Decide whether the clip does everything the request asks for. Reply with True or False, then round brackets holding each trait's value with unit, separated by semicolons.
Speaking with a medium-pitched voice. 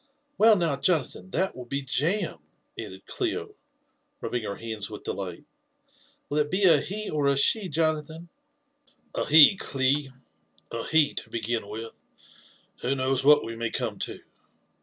True (145 Hz)